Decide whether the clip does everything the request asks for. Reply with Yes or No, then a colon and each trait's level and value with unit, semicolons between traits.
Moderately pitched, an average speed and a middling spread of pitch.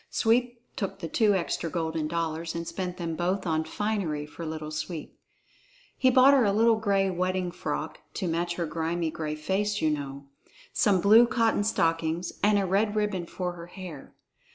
Yes: medium, 180 Hz; average, 175 wpm; average, 4.0 semitones